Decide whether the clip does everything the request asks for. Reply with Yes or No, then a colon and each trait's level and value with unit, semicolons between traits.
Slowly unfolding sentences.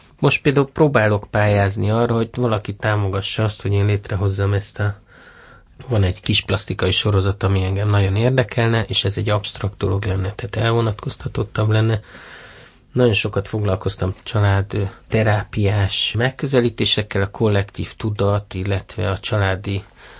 No: average, 130 wpm